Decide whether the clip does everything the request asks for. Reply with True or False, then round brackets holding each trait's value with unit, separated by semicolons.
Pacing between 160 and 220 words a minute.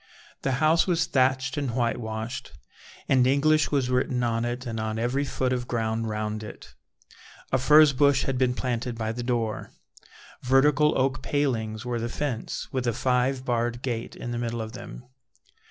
True (170 wpm)